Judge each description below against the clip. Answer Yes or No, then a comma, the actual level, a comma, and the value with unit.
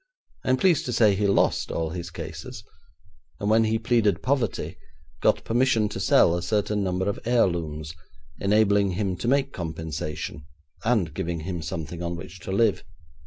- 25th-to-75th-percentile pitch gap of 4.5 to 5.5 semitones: Yes, average, 4.9 semitones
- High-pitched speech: No, low, 100 Hz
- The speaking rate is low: No, average, 165 wpm